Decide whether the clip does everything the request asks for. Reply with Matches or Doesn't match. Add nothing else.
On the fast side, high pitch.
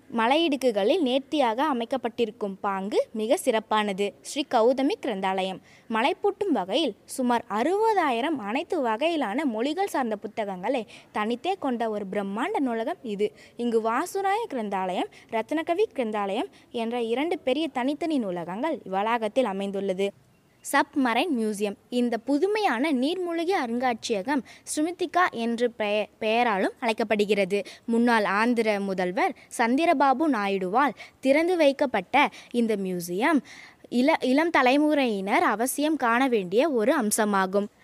Doesn't match